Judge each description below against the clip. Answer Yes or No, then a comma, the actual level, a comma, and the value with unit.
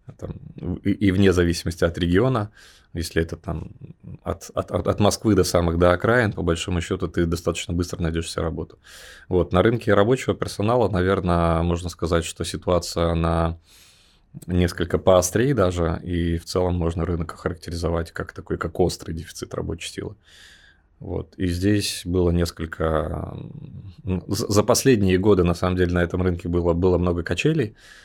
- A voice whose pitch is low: Yes, very low, 90 Hz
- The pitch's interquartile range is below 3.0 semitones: Yes, narrow, 2.5 semitones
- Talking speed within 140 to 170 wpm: Yes, average, 150 wpm